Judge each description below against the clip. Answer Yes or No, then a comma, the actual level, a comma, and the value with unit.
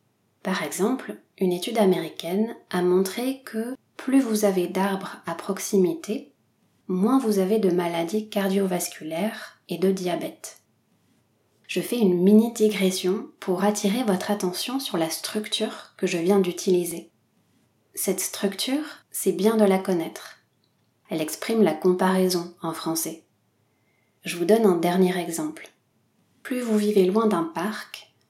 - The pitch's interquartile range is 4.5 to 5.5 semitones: No, average, 3.3 semitones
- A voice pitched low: No, high, 195 Hz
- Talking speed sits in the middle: No, slow, 135 wpm